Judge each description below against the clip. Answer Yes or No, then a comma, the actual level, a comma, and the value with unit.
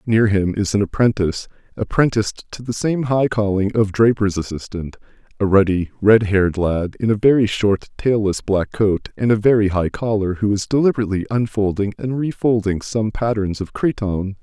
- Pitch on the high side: No, low, 105 Hz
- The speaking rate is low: No, average, 170 wpm